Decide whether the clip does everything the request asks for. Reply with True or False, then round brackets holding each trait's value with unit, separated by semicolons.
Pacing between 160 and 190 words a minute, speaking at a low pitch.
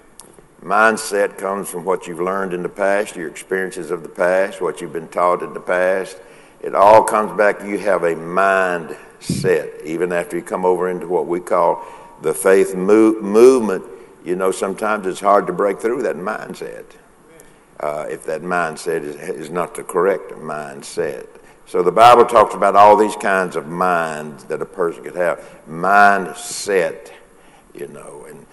True (170 wpm; 105 Hz)